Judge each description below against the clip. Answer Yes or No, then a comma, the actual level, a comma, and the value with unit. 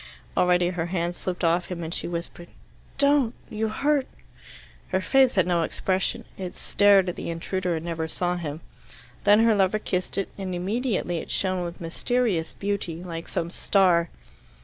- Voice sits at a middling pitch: Yes, medium, 180 Hz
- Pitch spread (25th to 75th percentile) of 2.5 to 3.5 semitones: Yes, average, 3.0 semitones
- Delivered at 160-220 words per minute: Yes, average, 170 wpm